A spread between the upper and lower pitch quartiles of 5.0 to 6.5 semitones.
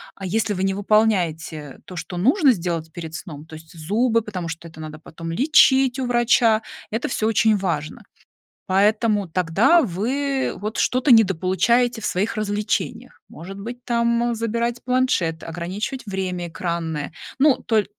Yes: wide, 5.5 semitones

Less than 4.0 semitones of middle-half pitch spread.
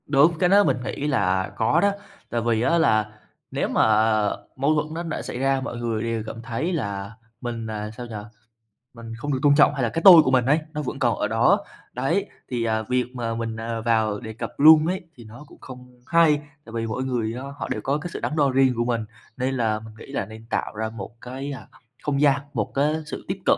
No: average, 4.4 semitones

